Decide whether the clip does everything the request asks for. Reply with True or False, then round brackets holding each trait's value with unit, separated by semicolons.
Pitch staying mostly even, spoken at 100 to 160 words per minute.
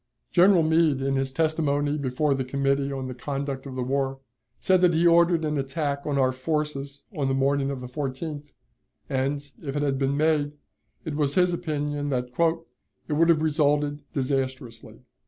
False (2.3 semitones; 175 wpm)